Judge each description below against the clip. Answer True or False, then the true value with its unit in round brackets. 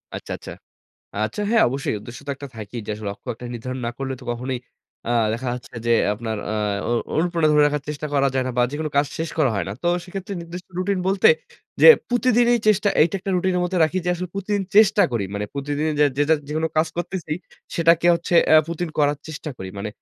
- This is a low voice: False (155 Hz)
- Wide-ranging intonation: True (5.9 semitones)